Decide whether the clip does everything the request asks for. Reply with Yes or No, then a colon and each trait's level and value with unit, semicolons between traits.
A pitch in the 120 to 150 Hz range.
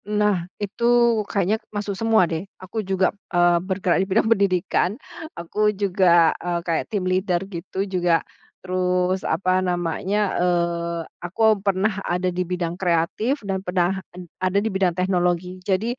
No: medium, 185 Hz